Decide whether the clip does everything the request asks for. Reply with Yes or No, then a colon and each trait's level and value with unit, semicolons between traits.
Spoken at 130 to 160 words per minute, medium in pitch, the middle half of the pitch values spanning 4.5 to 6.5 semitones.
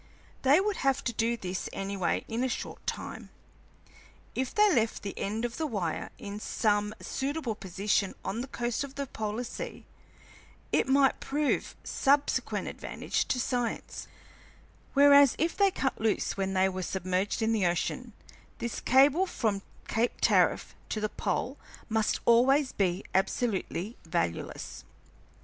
No: average, 150 wpm; high, 230 Hz; average, 5.2 semitones